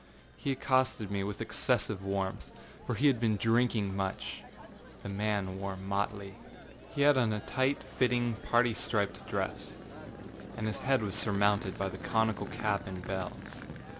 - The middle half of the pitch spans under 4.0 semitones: Yes, average, 3.4 semitones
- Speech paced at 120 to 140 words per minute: No, average, 155 wpm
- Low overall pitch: Yes, low, 105 Hz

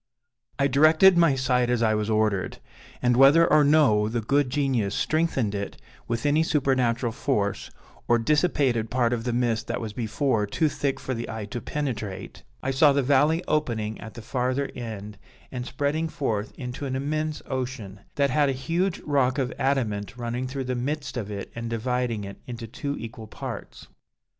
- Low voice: Yes, low, 125 Hz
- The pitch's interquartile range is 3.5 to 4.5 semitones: Yes, average, 4.0 semitones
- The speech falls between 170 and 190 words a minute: Yes, average, 180 wpm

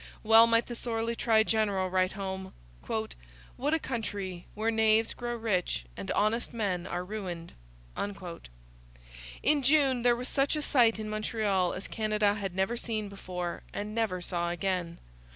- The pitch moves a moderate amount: Yes, average, 3.7 semitones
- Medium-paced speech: Yes, average, 150 wpm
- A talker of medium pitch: No, high, 215 Hz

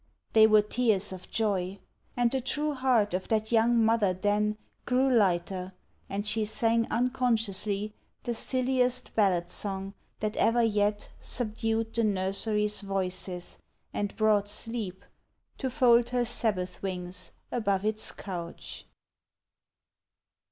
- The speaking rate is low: Yes, slow, 125 wpm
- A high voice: Yes, high, 215 Hz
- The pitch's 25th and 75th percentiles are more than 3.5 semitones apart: No, average, 3.1 semitones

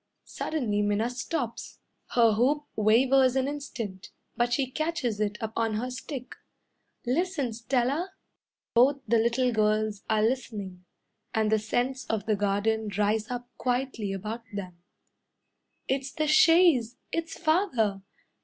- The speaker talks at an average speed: No, slow, 130 wpm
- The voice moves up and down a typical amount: Yes, average, 3.8 semitones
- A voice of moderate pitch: No, high, 235 Hz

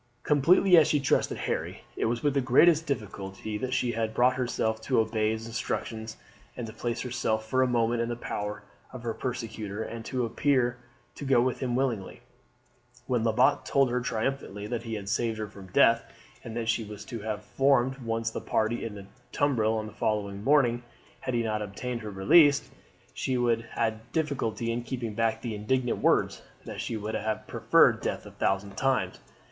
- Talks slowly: No, average, 190 wpm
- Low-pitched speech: Yes, low, 115 Hz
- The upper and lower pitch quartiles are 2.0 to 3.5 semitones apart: Yes, average, 2.9 semitones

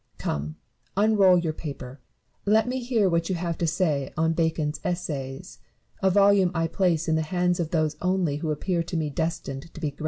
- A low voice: No, medium, 165 Hz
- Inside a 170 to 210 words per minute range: Yes, fast, 205 wpm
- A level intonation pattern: No, average, 3.2 semitones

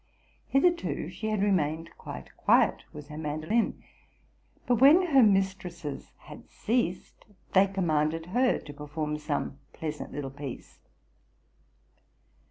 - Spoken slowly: Yes, slow, 120 wpm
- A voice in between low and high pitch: Yes, medium, 165 Hz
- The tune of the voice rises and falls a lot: Yes, wide, 6.2 semitones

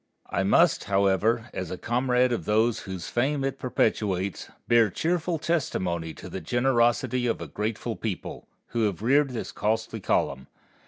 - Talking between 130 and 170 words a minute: Yes, average, 155 wpm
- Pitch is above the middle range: No, low, 115 Hz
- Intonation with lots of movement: No, average, 4.3 semitones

